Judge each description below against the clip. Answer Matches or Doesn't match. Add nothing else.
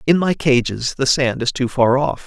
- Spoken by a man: Matches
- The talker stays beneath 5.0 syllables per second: Matches